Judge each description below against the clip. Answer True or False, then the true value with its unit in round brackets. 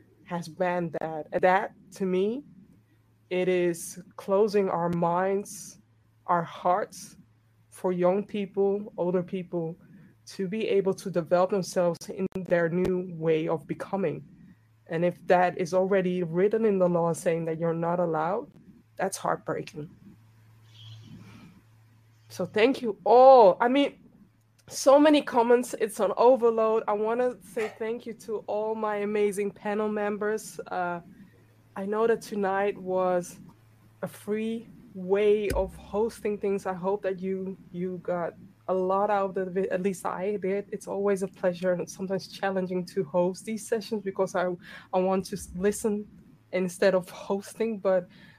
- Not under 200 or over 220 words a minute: False (150 wpm)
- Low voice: False (190 Hz)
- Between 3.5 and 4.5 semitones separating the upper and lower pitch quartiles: False (2.9 semitones)